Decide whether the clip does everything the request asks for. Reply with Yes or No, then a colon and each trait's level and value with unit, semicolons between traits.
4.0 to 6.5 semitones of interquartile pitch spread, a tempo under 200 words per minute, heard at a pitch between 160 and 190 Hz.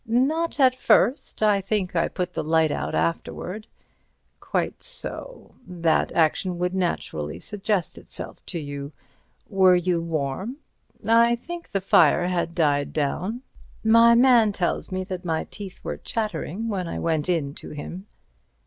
Yes: average, 5.1 semitones; average, 145 wpm; medium, 185 Hz